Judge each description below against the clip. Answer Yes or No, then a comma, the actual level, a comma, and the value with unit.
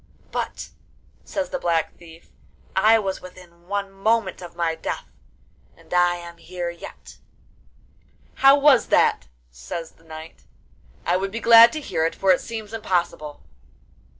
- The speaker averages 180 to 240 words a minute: No, average, 150 wpm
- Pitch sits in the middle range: Yes, medium, 180 Hz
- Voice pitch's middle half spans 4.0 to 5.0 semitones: Yes, average, 4.5 semitones